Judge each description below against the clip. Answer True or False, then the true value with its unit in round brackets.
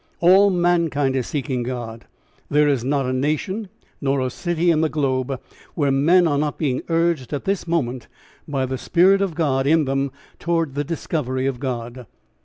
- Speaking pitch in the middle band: True (145 Hz)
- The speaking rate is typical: True (180 wpm)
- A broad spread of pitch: False (4.3 semitones)